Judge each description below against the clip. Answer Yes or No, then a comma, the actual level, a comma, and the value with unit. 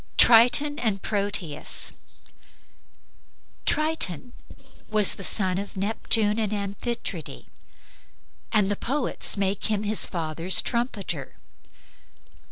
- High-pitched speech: Yes, high, 205 Hz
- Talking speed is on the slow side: Yes, slow, 90 wpm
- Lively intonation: No, average, 3.1 semitones